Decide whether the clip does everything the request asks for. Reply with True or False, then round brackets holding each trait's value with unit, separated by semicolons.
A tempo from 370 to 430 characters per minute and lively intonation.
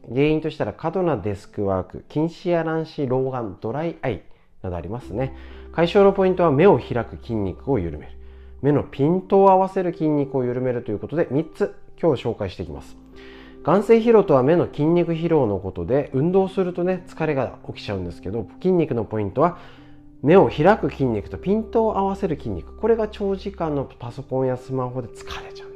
True (385 characters per minute; 8.5 semitones)